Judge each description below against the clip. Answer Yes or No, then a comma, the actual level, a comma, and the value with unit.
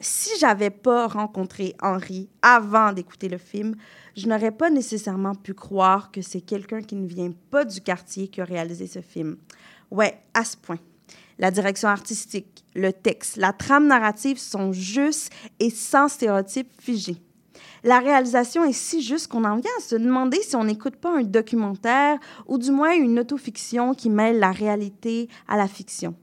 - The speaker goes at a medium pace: Yes, average, 175 wpm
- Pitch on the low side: No, high, 215 Hz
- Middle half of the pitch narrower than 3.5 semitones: No, average, 4.3 semitones